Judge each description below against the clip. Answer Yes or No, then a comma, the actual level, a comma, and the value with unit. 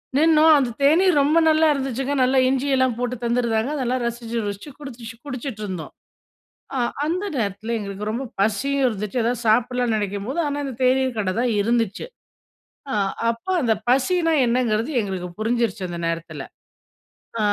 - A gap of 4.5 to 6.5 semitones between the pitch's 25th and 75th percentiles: No, average, 3.7 semitones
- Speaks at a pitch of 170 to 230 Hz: No, high, 240 Hz